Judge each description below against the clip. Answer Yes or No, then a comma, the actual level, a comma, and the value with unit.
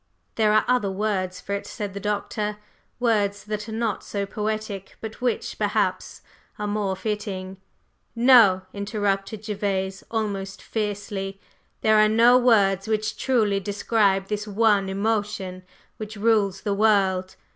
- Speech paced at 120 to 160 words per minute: Yes, average, 140 wpm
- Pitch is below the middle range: No, high, 205 Hz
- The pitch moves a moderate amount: No, narrow, 1.9 semitones